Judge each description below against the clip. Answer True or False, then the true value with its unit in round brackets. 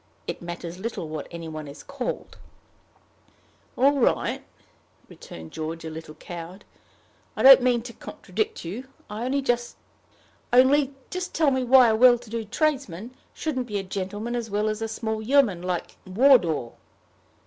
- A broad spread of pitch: True (6.5 semitones)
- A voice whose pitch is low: False (220 Hz)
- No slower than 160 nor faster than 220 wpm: False (150 wpm)